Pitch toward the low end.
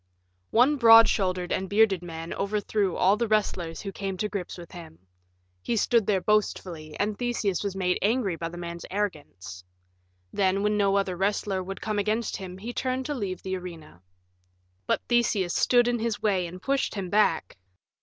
No: high, 195 Hz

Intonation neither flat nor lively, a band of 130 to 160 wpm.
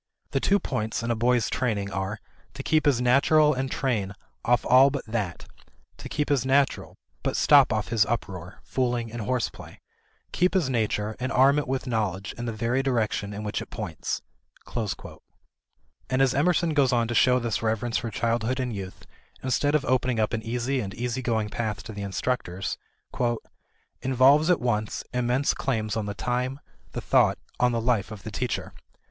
No: average, 3.3 semitones; average, 180 wpm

